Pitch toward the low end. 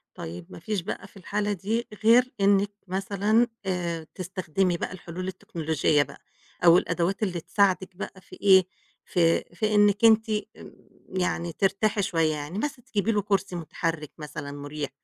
No: high, 190 Hz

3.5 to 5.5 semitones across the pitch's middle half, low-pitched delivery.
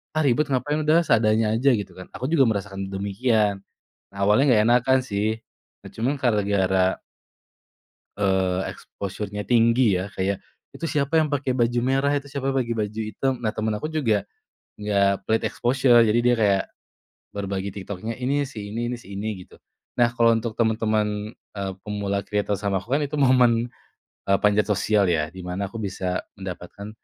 Yes: average, 3.8 semitones; low, 110 Hz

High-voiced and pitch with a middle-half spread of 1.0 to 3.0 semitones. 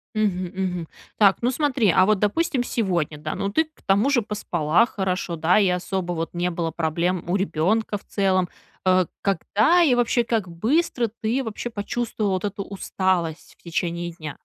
No: high, 195 Hz; average, 4.3 semitones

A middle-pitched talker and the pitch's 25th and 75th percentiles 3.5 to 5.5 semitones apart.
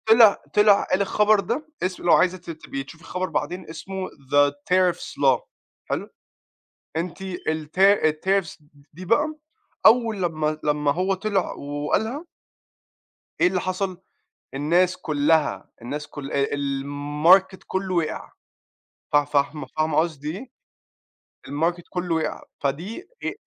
Yes: medium, 175 Hz; average, 4.3 semitones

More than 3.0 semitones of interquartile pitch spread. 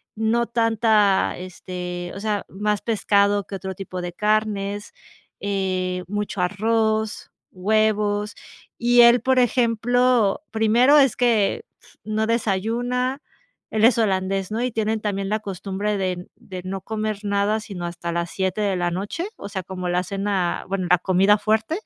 No: average, 2.7 semitones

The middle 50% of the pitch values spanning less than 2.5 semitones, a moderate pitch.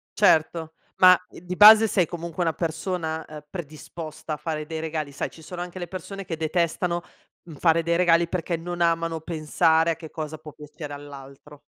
Yes: narrow, 2.1 semitones; medium, 165 Hz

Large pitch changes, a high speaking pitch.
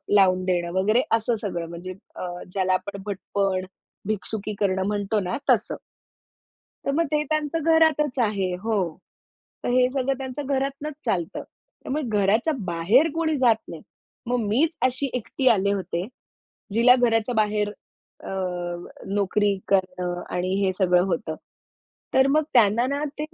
Yes: wide, 5.8 semitones; high, 210 Hz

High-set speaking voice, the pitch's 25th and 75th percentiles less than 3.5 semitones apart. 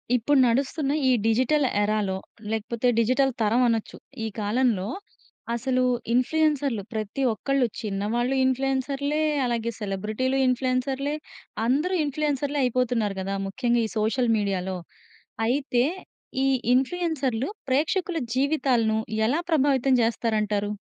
No: very high, 250 Hz; average, 3.8 semitones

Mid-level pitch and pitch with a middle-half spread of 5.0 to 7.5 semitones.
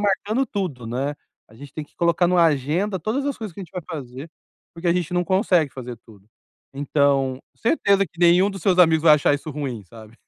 Yes: medium, 165 Hz; wide, 5.4 semitones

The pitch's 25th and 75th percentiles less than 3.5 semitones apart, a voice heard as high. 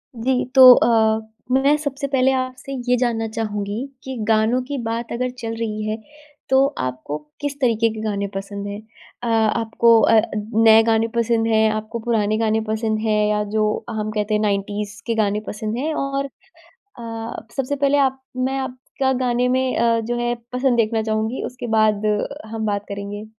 Yes: average, 3.0 semitones; high, 225 Hz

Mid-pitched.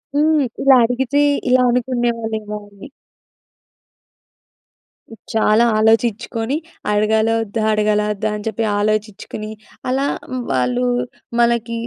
No: high, 220 Hz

